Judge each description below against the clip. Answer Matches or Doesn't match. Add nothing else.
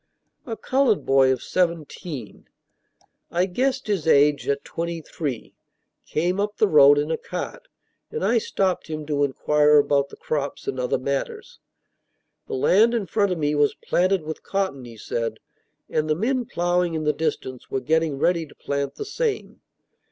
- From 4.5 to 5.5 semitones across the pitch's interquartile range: Matches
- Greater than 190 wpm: Doesn't match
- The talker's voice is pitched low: Doesn't match